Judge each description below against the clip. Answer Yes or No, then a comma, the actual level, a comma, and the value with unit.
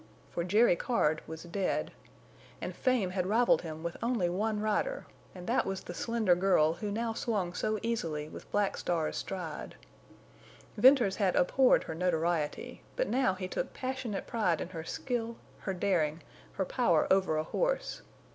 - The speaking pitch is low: No, high, 190 Hz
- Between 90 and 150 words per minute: No, average, 165 wpm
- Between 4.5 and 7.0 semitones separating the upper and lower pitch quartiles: Yes, average, 5.2 semitones